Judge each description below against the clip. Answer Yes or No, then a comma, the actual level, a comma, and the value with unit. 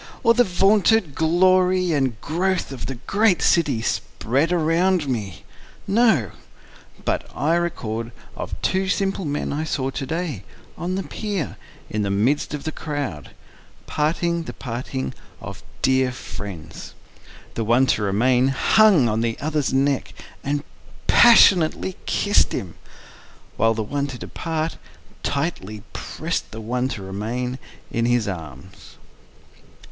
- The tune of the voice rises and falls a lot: Yes, wide, 7.0 semitones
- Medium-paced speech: No, slow, 125 wpm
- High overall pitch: No, medium, 140 Hz